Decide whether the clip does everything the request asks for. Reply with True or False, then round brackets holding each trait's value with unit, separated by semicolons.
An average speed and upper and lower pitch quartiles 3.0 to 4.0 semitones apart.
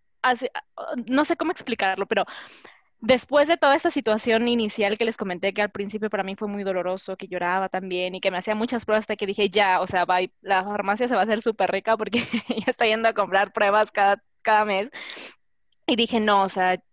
False (215 wpm; 3.4 semitones)